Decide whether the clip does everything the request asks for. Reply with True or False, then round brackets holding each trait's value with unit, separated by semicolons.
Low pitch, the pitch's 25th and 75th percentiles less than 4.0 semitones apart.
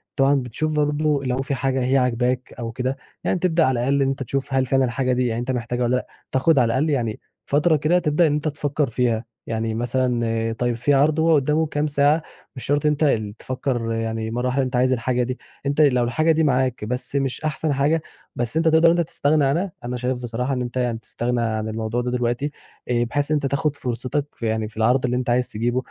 True (130 Hz; 3.2 semitones)